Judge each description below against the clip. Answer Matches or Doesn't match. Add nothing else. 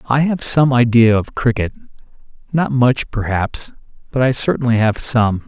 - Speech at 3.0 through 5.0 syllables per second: Matches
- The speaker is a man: Matches